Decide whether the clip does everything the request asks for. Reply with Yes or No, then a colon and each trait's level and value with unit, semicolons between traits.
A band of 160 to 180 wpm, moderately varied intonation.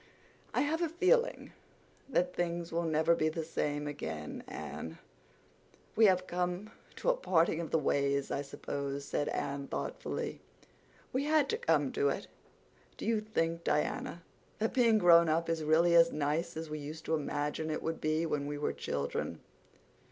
Yes: average, 170 wpm; average, 3.7 semitones